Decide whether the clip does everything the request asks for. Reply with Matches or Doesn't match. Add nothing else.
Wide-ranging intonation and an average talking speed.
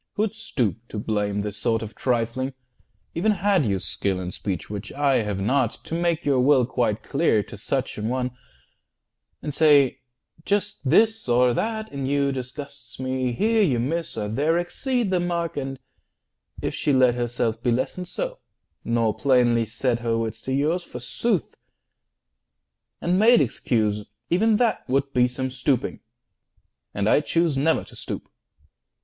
Matches